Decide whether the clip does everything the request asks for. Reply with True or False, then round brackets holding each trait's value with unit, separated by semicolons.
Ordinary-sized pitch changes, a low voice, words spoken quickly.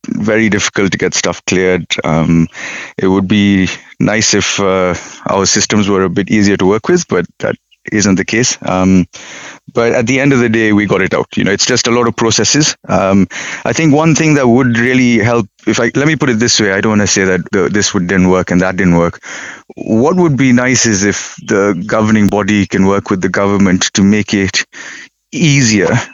True (4.0 semitones; 105 Hz; 220 wpm)